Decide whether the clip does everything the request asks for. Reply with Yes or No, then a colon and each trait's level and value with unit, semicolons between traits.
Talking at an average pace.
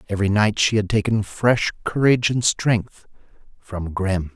Yes: average, 150 wpm